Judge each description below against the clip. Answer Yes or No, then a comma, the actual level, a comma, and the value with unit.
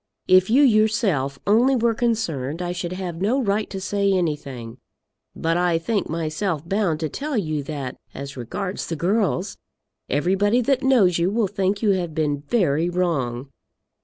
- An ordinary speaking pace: Yes, average, 165 wpm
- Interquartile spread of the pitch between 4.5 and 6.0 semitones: Yes, average, 5.2 semitones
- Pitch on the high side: No, medium, 180 Hz